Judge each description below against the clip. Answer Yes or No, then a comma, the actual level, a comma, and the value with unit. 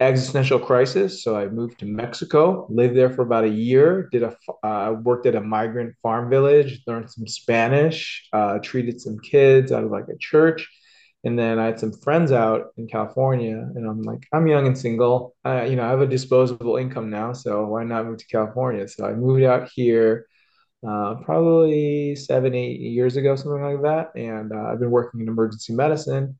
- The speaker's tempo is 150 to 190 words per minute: No, average, 200 wpm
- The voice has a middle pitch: No, low, 125 Hz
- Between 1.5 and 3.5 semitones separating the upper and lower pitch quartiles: Yes, average, 3.2 semitones